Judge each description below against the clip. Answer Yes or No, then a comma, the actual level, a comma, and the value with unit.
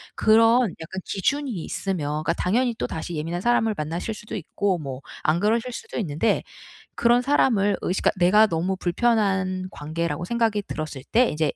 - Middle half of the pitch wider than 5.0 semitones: Yes, wide, 5.6 semitones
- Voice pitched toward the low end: No, high, 190 Hz